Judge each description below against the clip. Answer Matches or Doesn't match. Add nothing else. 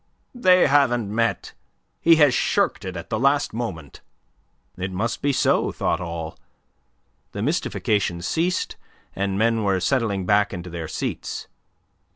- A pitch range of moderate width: Doesn't match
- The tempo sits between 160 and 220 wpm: Doesn't match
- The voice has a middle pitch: Doesn't match